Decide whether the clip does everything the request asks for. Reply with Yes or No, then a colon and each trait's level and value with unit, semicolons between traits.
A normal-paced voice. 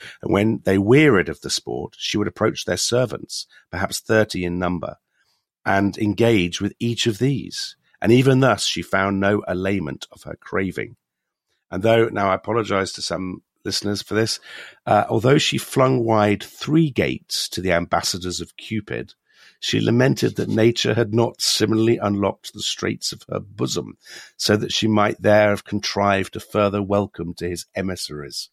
Yes: average, 170 wpm